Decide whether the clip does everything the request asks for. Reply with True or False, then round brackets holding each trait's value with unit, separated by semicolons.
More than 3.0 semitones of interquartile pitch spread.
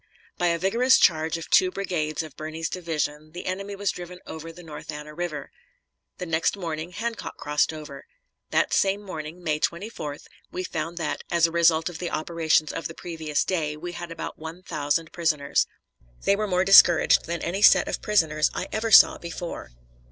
False (2.6 semitones)